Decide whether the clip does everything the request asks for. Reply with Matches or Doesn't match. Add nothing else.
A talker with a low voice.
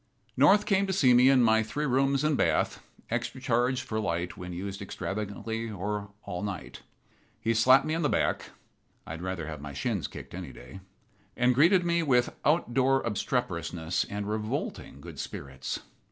Matches